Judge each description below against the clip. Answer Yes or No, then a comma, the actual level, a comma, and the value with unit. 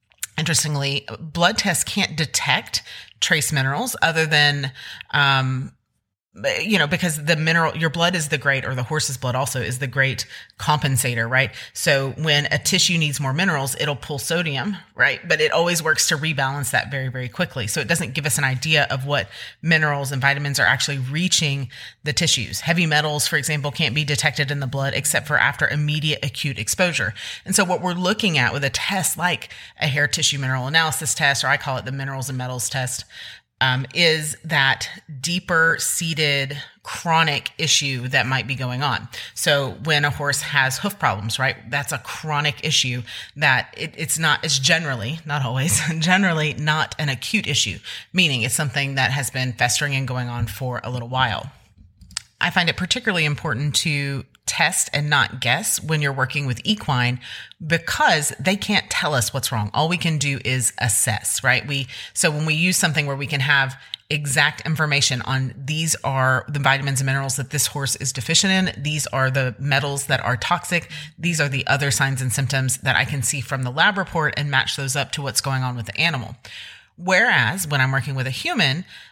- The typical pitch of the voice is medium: Yes, medium, 145 Hz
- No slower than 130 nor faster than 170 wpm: No, average, 195 wpm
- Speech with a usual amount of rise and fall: Yes, average, 3.2 semitones